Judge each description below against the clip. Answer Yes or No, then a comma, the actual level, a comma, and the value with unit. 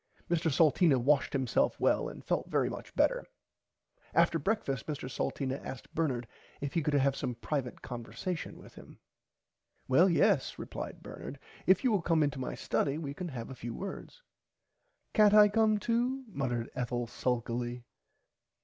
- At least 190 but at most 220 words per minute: No, average, 160 wpm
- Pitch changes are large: Yes, wide, 6.4 semitones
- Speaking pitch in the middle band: Yes, medium, 145 Hz